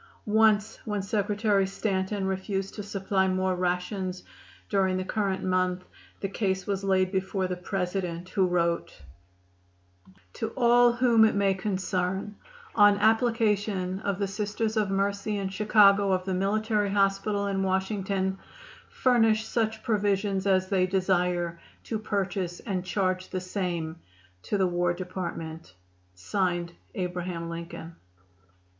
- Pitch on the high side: Yes, high, 195 Hz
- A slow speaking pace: Yes, slow, 125 wpm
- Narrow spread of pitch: Yes, narrow, 2.0 semitones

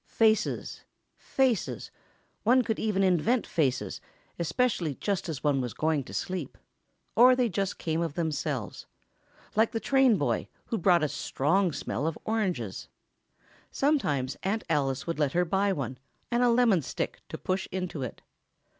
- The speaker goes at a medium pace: Yes, average, 150 wpm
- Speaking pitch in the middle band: Yes, medium, 180 Hz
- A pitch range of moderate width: No, wide, 6.9 semitones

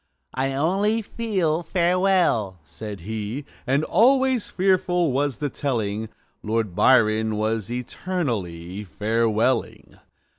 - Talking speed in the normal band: No, slow, 100 wpm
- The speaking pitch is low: Yes, low, 130 Hz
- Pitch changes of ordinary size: No, wide, 8.6 semitones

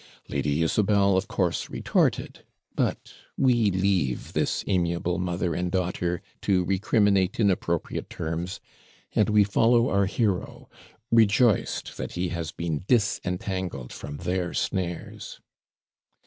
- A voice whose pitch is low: Yes, very low, 90 Hz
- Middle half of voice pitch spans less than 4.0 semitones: Yes, average, 2.8 semitones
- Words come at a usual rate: No, slow, 120 wpm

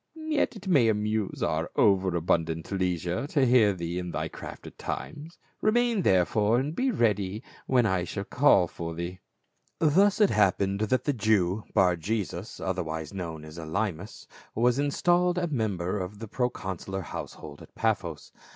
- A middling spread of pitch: No, wide, 6.8 semitones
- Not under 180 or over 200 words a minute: No, average, 165 wpm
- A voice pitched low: Yes, low, 105 Hz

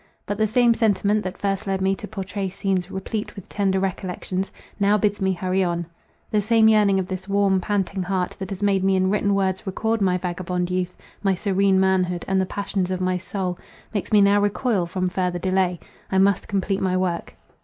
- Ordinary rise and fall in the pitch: No, narrow, 1.6 semitones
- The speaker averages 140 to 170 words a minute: No, fast, 205 wpm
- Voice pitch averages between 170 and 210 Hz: Yes, high, 190 Hz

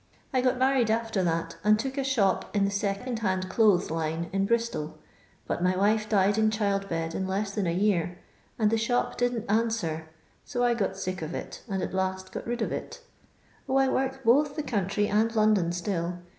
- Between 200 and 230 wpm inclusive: Yes, fast, 205 wpm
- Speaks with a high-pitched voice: Yes, high, 205 Hz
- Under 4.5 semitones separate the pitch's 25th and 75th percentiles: Yes, average, 3.8 semitones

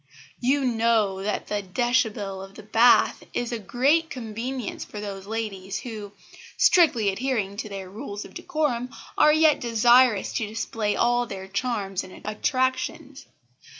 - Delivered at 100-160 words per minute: Yes, average, 145 wpm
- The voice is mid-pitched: No, high, 225 Hz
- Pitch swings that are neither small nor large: Yes, average, 3.9 semitones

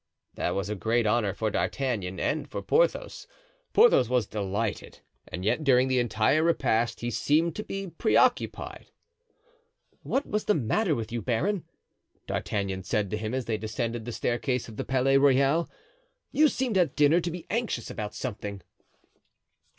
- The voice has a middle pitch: No, low, 125 Hz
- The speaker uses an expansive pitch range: Yes, wide, 6.6 semitones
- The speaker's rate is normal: Yes, average, 160 wpm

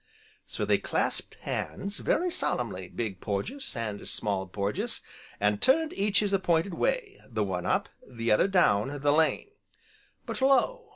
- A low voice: No, medium, 145 Hz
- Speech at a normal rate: Yes, average, 150 wpm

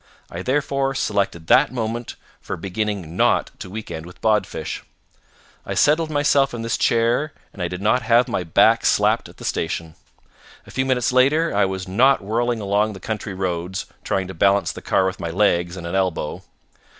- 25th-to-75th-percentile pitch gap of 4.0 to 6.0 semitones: Yes, average, 5.1 semitones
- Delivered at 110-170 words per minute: No, average, 185 wpm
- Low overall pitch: Yes, low, 105 Hz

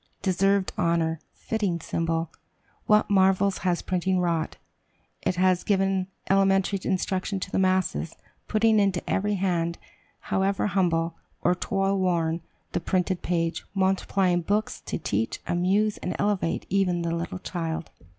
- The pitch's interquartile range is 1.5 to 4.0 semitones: Yes, narrow, 2.4 semitones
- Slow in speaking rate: Yes, slow, 130 wpm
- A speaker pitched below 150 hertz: No, medium, 185 Hz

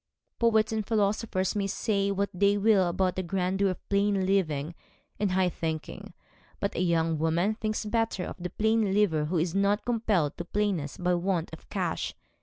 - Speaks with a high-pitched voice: Yes, high, 195 Hz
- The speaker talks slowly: No, average, 180 wpm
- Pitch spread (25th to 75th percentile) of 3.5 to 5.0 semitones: No, average, 3.1 semitones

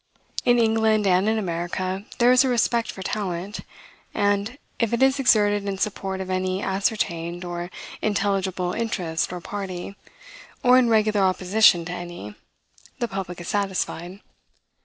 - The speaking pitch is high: Yes, high, 195 Hz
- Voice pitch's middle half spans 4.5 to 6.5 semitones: No, average, 3.4 semitones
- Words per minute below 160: Yes, average, 145 wpm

